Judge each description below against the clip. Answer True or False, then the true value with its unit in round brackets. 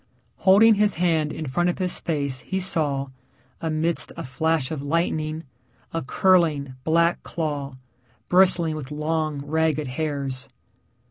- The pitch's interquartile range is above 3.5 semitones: False (3.1 semitones)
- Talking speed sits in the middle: False (130 wpm)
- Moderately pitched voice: True (155 Hz)